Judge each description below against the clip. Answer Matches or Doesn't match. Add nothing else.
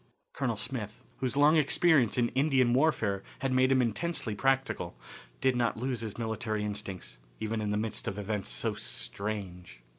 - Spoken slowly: Doesn't match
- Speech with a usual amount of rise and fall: Matches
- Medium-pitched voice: Doesn't match